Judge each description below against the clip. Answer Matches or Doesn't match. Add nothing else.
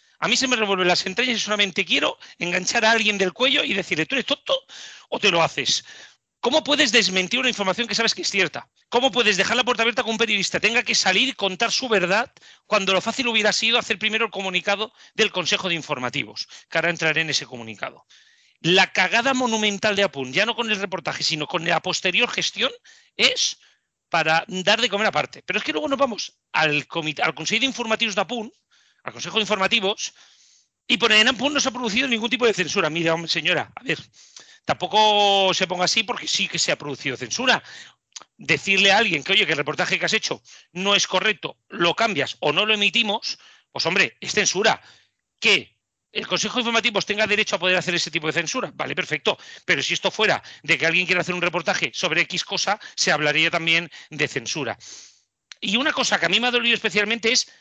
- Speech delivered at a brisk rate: Matches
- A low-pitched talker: Doesn't match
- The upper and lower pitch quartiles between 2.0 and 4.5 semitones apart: Doesn't match